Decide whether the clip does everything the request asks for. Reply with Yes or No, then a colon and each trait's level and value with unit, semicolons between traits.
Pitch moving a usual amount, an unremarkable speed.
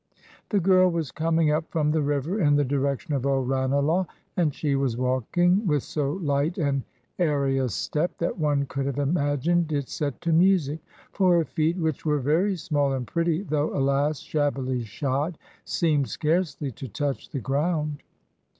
Yes: average, 3.2 semitones; average, 170 wpm